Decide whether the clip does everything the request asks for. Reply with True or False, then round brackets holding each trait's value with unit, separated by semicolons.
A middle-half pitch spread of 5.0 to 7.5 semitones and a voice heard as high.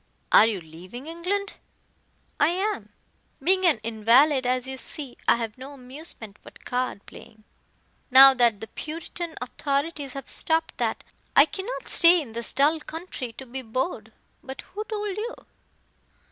True (5.6 semitones; 275 Hz)